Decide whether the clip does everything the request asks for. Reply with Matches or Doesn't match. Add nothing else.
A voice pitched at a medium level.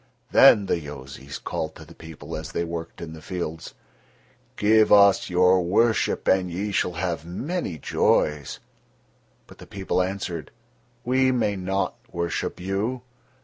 Doesn't match